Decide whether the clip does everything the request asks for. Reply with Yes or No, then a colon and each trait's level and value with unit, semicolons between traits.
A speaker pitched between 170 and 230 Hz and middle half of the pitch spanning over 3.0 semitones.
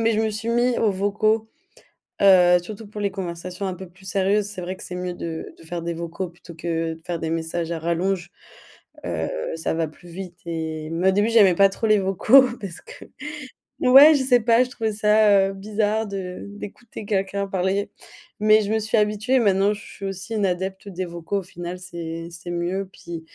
Yes: high, 190 Hz; average, 3.5 semitones